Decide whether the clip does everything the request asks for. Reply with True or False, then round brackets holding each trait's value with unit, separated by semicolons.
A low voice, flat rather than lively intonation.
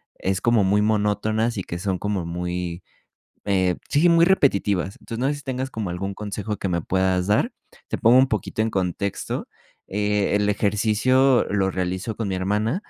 False (105 Hz; 3.1 semitones)